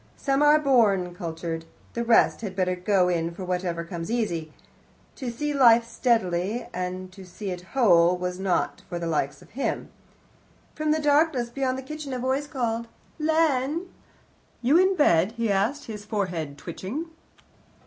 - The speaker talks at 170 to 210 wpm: No, average, 160 wpm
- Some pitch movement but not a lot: No, wide, 7.1 semitones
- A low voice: No, high, 220 Hz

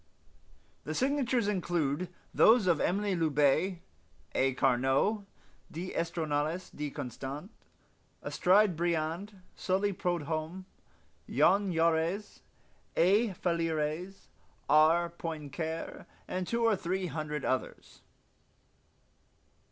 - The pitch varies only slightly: No, average, 3.8 semitones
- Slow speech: Yes, slow, 85 wpm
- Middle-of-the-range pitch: Yes, medium, 170 Hz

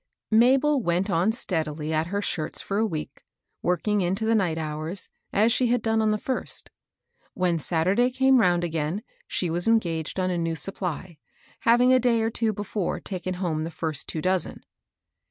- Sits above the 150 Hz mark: Yes, medium, 185 Hz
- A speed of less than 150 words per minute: No, average, 180 wpm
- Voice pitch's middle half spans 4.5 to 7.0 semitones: Yes, average, 5.1 semitones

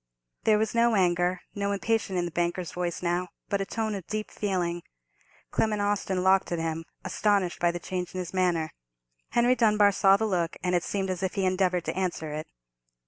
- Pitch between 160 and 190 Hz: Yes, medium, 185 Hz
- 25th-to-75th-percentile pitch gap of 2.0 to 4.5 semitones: Yes, average, 2.7 semitones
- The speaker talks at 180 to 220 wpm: Yes, average, 200 wpm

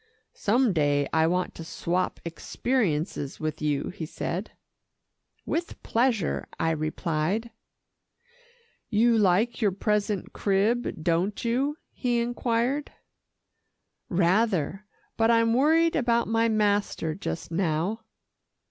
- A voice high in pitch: Yes, high, 205 Hz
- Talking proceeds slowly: Yes, slow, 105 wpm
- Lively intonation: Yes, wide, 5.9 semitones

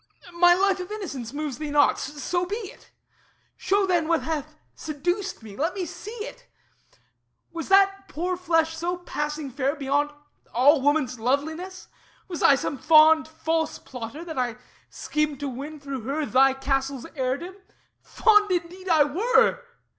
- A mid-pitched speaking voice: No, very high, 315 Hz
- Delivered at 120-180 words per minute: Yes, average, 155 wpm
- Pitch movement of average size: Yes, average, 4.3 semitones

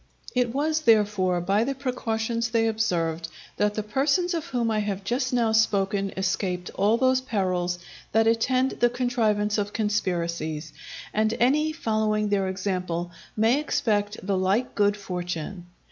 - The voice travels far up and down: No, average, 4.0 semitones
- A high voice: Yes, high, 215 Hz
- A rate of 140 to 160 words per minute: Yes, average, 145 wpm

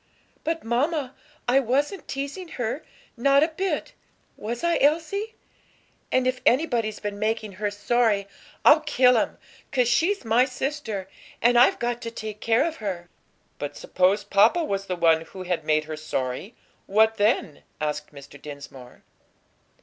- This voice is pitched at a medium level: No, high, 230 Hz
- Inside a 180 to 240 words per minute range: No, average, 150 wpm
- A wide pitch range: Yes, wide, 6.1 semitones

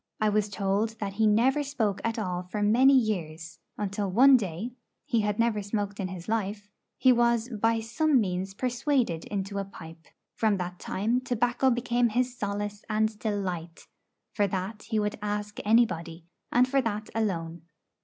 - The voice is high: Yes, high, 210 Hz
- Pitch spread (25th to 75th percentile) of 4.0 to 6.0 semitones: No, average, 3.3 semitones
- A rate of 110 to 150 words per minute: No, average, 165 wpm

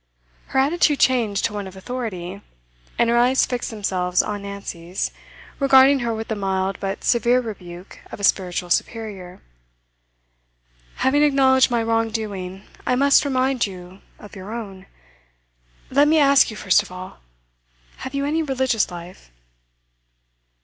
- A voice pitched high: Yes, high, 220 Hz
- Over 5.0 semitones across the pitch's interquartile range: Yes, wide, 5.5 semitones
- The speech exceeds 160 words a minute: No, average, 145 wpm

